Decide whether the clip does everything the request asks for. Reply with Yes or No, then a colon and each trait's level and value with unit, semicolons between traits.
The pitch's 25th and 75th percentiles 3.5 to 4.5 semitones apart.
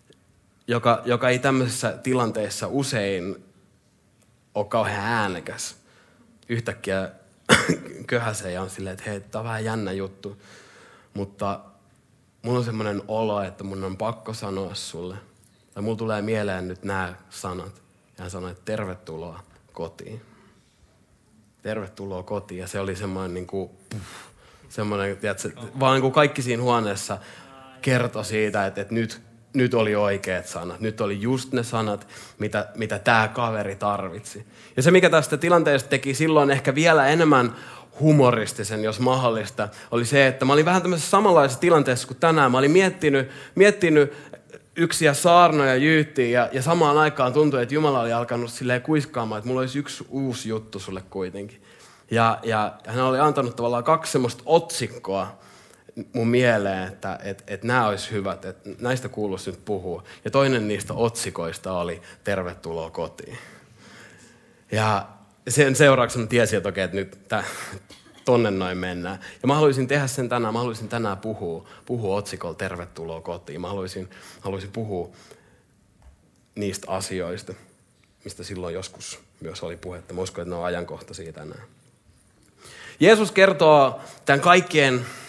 No: average, 4.9 semitones